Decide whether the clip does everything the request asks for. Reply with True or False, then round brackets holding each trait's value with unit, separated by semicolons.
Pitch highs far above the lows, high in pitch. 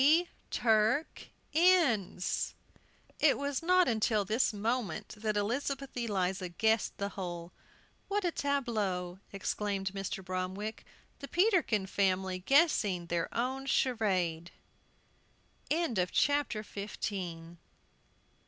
True (6.2 semitones; 215 Hz)